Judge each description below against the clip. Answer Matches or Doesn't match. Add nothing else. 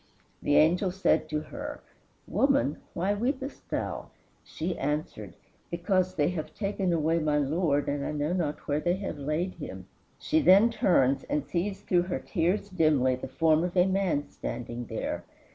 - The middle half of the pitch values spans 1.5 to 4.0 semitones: Doesn't match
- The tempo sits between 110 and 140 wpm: Doesn't match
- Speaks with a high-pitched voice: Doesn't match